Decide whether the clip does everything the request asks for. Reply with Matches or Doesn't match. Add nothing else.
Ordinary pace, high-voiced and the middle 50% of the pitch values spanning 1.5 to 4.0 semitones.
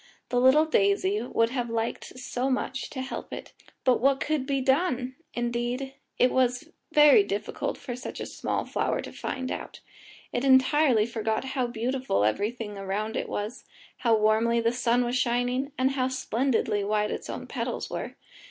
Matches